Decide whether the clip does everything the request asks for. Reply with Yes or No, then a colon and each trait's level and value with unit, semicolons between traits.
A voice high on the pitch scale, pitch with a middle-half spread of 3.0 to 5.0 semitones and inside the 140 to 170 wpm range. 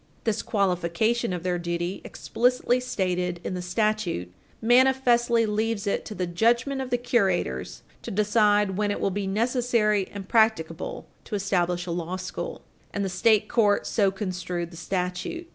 Yes: high, 205 Hz; average, 4.1 semitones; average, 160 wpm